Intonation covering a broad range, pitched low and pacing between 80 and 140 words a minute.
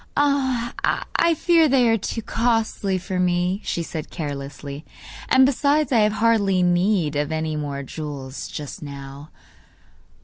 No: wide, 8.0 semitones; medium, 185 Hz; slow, 135 wpm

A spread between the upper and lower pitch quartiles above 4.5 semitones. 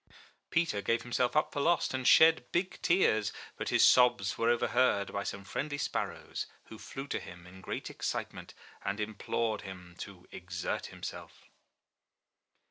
Yes: wide, 5.5 semitones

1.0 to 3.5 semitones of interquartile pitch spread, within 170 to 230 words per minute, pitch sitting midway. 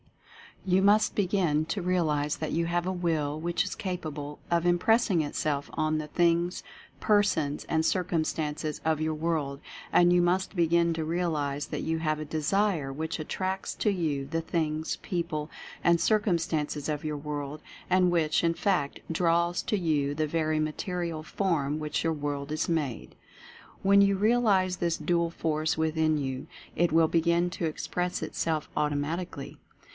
No: narrow, 2.6 semitones; average, 160 wpm; medium, 165 Hz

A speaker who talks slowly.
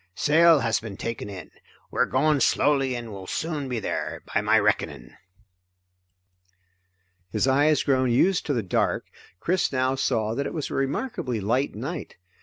No: average, 165 wpm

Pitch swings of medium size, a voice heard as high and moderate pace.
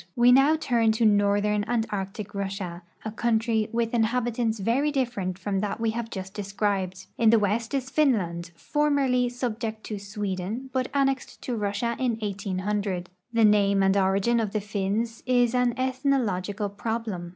Yes: average, 3.3 semitones; high, 220 Hz; average, 160 wpm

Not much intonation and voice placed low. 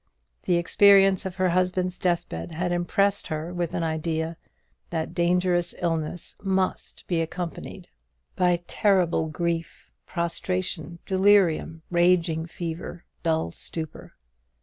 No: narrow, 1.9 semitones; medium, 175 Hz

